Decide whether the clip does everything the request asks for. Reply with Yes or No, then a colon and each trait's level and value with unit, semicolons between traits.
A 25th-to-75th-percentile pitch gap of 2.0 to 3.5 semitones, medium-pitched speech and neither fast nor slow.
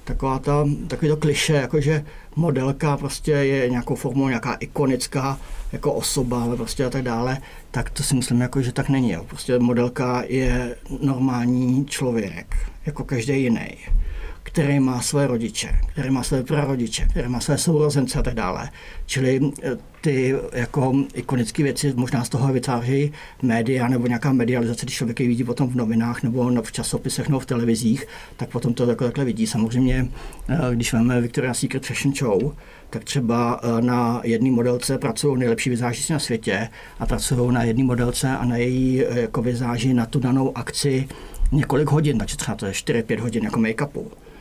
No: narrow, 2.4 semitones; low, 125 Hz; average, 160 wpm